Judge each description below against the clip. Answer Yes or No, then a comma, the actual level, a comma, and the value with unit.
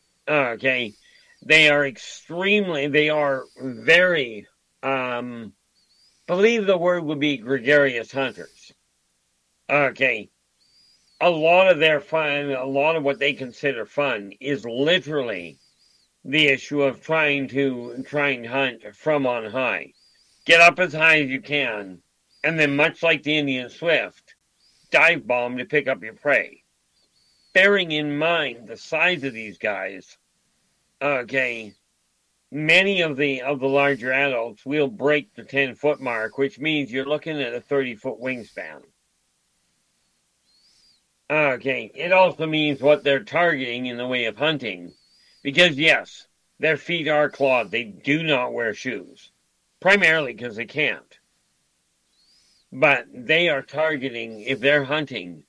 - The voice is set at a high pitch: No, low, 135 Hz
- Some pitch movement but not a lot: Yes, average, 4.0 semitones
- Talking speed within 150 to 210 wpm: No, slow, 135 wpm